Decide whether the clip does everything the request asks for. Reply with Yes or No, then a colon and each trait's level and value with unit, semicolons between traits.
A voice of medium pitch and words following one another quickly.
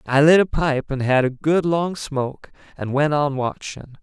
Yes: medium, 145 Hz; fast, 210 wpm